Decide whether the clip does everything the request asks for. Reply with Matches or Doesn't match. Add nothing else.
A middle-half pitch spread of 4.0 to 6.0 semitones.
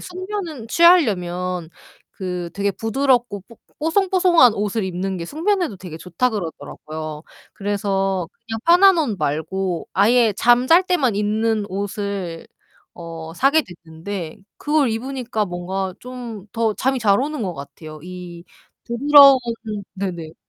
Doesn't match